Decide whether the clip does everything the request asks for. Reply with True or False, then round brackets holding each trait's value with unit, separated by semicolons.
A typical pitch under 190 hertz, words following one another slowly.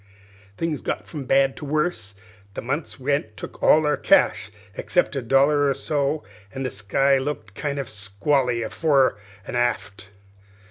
False (135 Hz; 155 wpm)